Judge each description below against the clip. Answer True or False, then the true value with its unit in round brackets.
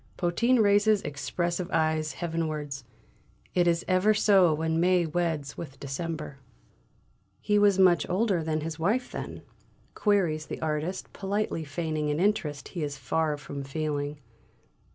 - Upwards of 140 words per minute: False (135 wpm)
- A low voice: False (165 Hz)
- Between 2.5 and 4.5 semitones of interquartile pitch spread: True (3.6 semitones)